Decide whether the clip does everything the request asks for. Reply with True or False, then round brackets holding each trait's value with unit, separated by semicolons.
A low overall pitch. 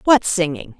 False (180 Hz)